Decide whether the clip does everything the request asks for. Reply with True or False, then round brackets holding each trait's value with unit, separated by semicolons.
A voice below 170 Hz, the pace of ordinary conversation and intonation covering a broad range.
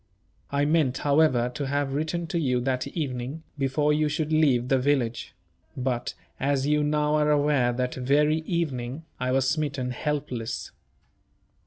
False (140 Hz; 150 wpm; 2.9 semitones)